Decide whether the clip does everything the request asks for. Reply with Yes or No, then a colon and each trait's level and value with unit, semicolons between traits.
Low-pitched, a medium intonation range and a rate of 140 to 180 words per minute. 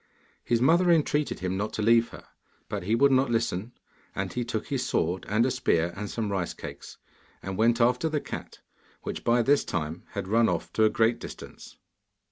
No: low, 115 Hz; average, 4.2 semitones; average, 200 wpm